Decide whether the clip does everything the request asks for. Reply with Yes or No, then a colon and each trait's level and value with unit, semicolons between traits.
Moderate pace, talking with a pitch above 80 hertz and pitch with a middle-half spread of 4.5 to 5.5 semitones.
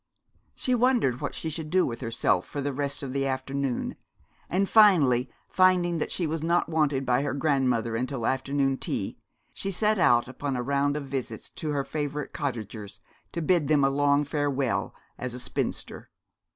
No: average, 180 wpm; medium, 140 Hz; average, 3.4 semitones